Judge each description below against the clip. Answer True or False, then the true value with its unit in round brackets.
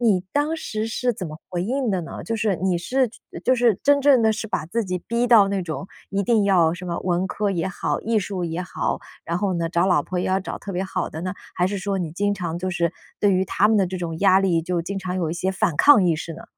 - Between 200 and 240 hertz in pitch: False (190 Hz)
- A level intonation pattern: False (3.4 semitones)